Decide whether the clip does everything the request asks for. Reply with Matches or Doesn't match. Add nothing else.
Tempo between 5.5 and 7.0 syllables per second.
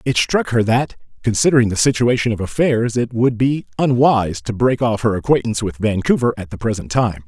Matches